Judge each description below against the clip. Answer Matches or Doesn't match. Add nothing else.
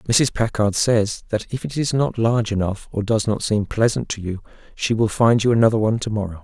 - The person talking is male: Matches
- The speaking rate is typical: Doesn't match